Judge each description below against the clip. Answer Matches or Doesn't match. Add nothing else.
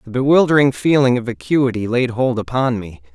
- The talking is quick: Doesn't match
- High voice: Doesn't match